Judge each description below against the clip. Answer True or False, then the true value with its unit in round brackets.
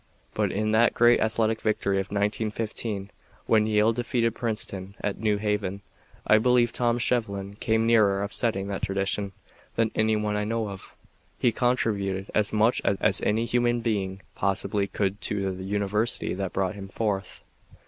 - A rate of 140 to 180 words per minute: True (160 wpm)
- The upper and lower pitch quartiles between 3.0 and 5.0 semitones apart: False (2.4 semitones)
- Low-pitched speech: True (105 Hz)